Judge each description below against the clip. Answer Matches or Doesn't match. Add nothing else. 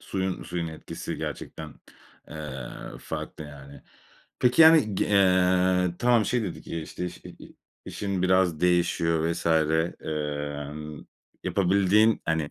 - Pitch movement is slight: Doesn't match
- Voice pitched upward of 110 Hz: Doesn't match